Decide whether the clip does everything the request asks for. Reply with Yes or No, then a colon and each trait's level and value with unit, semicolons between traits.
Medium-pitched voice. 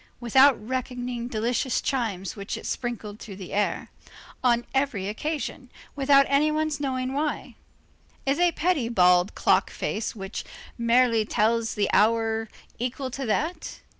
No: high, 240 Hz